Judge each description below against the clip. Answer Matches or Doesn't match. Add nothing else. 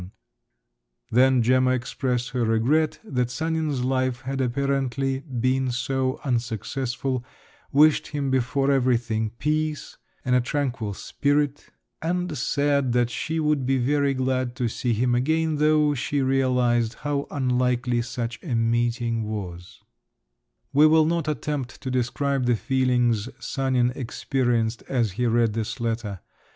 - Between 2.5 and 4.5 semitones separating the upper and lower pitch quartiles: Matches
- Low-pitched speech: Matches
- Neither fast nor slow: Doesn't match